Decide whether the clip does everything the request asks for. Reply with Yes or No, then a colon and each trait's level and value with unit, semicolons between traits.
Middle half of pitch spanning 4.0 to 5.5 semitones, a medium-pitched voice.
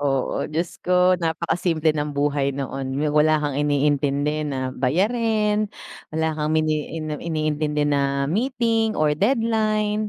Yes: average, 4.4 semitones; medium, 155 Hz